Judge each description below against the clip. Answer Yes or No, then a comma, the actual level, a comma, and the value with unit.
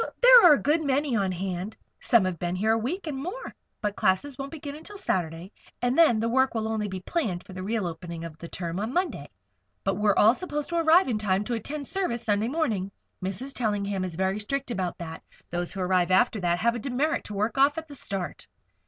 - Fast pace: Yes, fast, 230 wpm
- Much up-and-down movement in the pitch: Yes, wide, 6.9 semitones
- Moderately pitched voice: No, high, 220 Hz